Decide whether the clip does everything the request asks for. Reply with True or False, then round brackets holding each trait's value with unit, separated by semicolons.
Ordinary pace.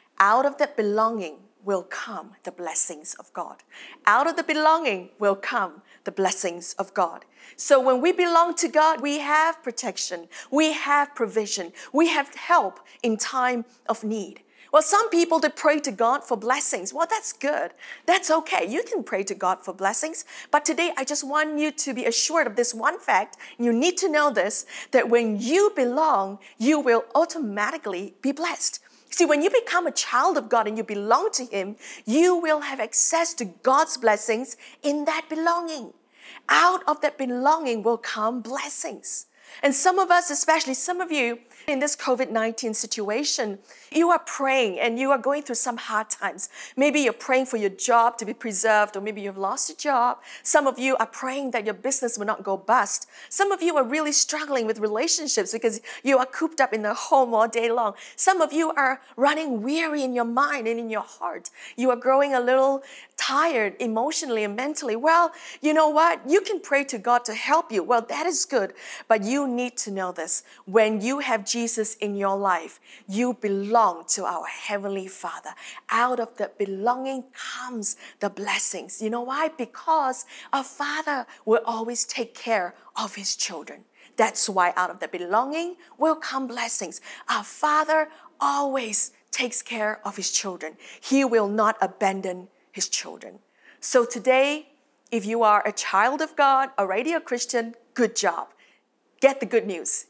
True (180 wpm)